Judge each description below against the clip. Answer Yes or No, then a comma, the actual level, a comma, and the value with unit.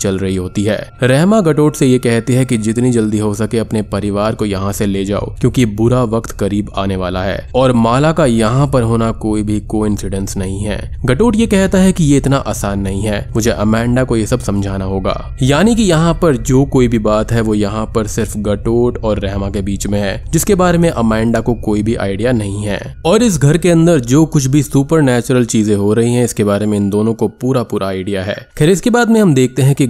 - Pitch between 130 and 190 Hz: No, low, 115 Hz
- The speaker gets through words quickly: Yes, fast, 235 wpm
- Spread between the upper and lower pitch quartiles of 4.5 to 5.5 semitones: Yes, average, 4.8 semitones